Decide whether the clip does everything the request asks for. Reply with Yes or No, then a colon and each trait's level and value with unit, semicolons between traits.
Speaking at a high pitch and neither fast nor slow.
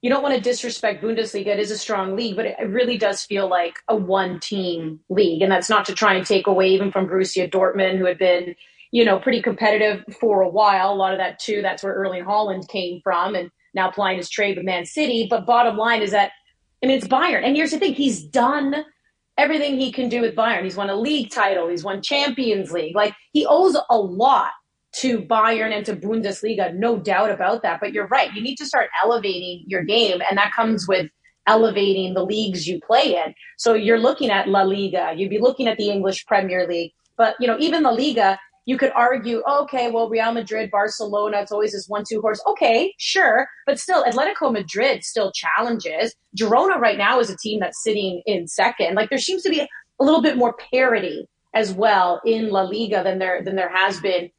No: high, 210 Hz; fast, 220 wpm